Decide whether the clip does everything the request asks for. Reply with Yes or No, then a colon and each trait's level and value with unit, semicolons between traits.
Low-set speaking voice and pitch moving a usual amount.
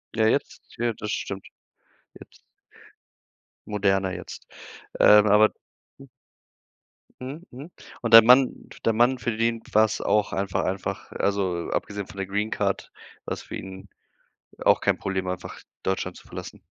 Yes: low, 105 Hz; average, 3.0 semitones